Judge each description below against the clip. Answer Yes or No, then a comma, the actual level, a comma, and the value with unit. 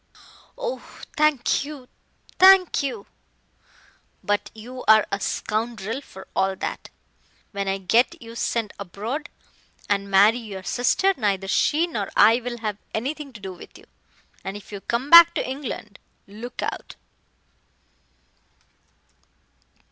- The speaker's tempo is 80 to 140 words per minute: Yes, slow, 135 wpm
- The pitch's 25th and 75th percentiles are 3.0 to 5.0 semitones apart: No, wide, 5.4 semitones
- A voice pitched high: Yes, high, 230 Hz